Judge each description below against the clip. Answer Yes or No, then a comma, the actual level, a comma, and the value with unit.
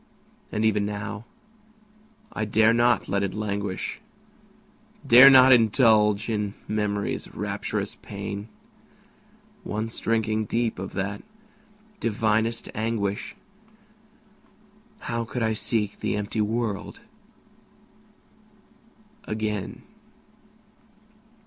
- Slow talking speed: Yes, slow, 85 wpm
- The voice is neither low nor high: No, low, 110 Hz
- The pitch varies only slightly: Yes, narrow, 1.9 semitones